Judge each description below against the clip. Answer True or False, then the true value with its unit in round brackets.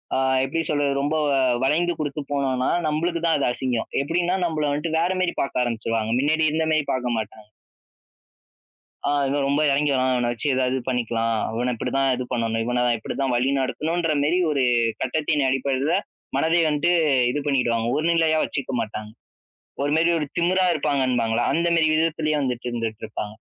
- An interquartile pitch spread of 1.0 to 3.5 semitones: False (4.2 semitones)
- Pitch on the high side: False (140 Hz)